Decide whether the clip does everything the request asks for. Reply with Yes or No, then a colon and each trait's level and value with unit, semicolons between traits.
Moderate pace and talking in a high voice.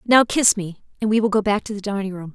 No: fast, 305 wpm; high, 205 Hz